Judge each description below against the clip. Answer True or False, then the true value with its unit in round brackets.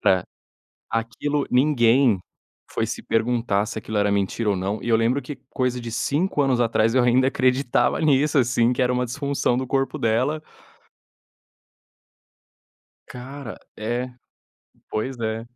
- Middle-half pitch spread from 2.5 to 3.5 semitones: True (3.0 semitones)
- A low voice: True (125 Hz)